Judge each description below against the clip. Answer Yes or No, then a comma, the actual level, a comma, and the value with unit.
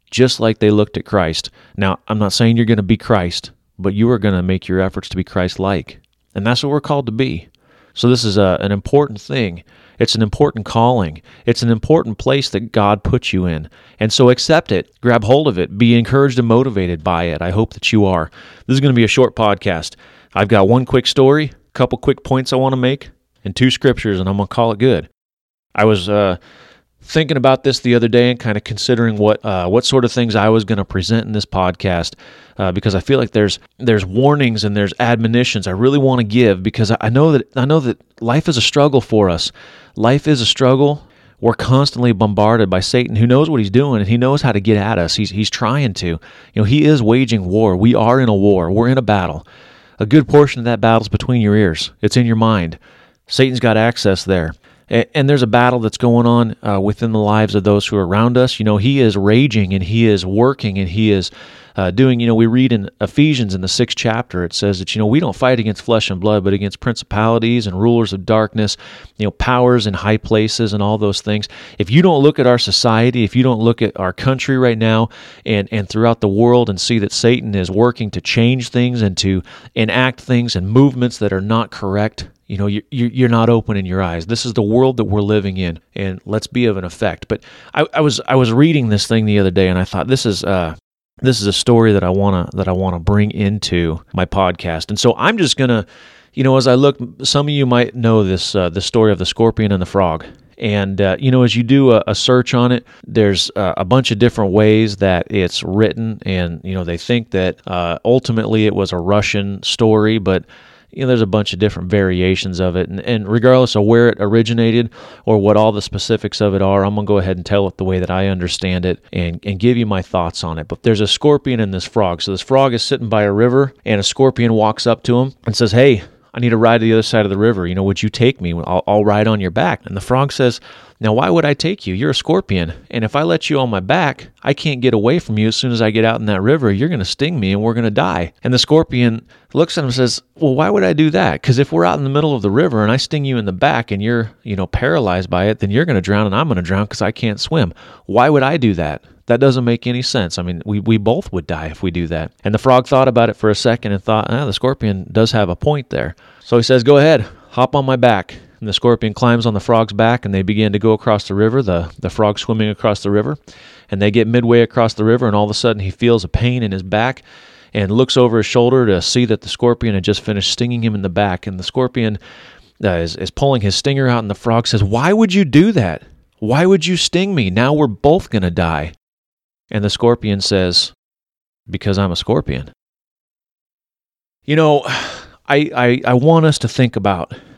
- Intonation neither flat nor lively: Yes, average, 3.8 semitones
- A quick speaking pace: Yes, fast, 255 wpm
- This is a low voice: Yes, low, 110 Hz